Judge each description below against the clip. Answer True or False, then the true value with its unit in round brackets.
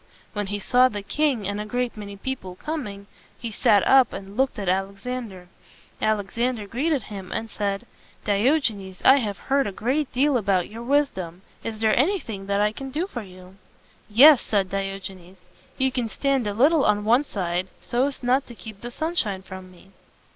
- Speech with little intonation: False (4.8 semitones)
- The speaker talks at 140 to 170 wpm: False (185 wpm)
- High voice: True (215 Hz)